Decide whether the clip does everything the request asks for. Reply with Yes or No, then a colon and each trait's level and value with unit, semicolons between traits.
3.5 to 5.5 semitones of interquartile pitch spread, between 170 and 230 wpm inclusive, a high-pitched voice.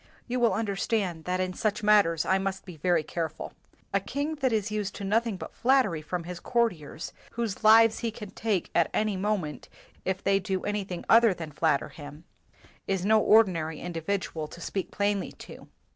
Yes: average, 4.0 semitones; average, 185 wpm; high, 195 Hz